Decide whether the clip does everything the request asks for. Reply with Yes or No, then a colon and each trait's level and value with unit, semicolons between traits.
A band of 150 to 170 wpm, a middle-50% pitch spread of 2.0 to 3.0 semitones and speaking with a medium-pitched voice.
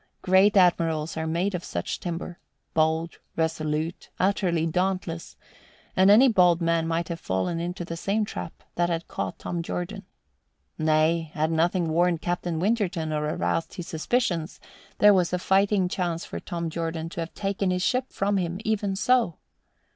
Yes: average, 160 wpm; average, 2.7 semitones; medium, 175 Hz